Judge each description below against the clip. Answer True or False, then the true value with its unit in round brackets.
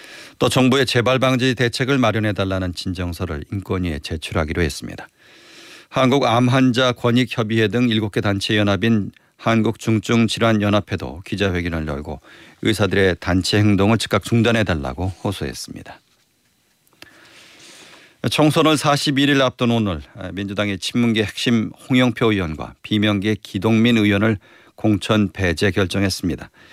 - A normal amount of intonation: True (4.0 semitones)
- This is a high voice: False (105 Hz)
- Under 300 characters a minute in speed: False (305 characters per minute)